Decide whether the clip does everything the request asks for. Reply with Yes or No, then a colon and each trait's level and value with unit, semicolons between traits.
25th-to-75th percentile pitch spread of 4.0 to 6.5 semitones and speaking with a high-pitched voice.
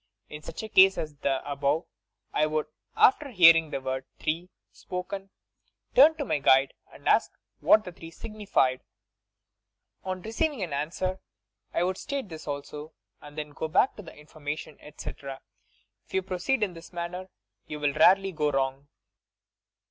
No: average, 4.5 semitones; medium, 165 Hz